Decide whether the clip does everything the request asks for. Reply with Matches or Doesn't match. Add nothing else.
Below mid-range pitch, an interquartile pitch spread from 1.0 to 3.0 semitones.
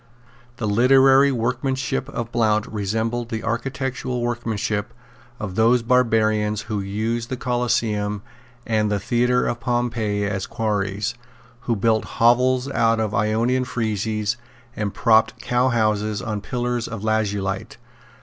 Matches